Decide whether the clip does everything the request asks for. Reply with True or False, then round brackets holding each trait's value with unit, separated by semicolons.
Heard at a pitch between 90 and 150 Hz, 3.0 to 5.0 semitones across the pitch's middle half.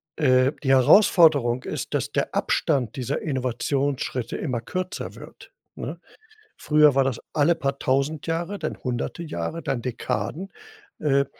True (140 Hz; 3.6 semitones)